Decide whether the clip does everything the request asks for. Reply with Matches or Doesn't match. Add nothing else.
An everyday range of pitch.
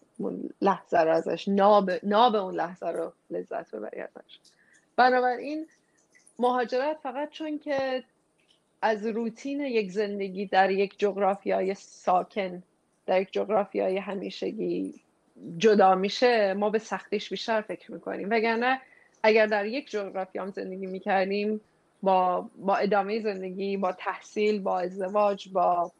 Matches